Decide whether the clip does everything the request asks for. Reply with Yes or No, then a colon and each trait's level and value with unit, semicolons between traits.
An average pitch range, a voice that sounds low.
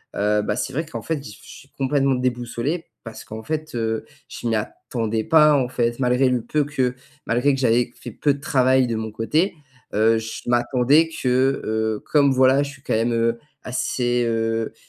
Yes: average, 3.2 semitones; low, 125 Hz